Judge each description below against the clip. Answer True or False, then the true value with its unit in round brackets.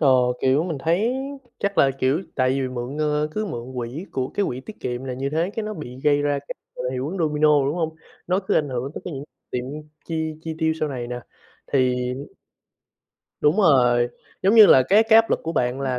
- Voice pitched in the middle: True (145 Hz)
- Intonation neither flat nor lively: True (4.2 semitones)